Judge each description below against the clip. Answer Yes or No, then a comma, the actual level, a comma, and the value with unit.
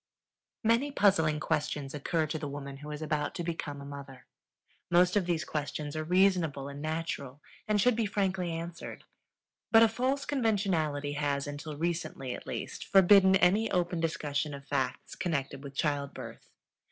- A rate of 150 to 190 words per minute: Yes, average, 160 wpm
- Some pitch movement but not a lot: Yes, average, 4.6 semitones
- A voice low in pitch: No, medium, 160 Hz